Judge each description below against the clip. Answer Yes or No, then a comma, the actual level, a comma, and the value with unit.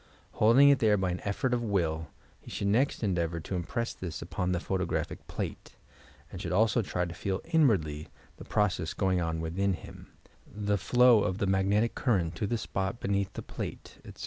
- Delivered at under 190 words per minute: No, average, 195 wpm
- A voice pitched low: Yes, very low, 95 Hz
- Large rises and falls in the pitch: No, average, 3.7 semitones